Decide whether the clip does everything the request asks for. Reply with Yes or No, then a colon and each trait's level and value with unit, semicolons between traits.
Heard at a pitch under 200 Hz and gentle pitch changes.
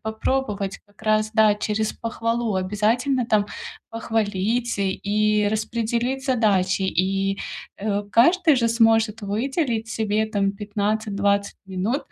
No: high, 215 Hz; narrow, 2.3 semitones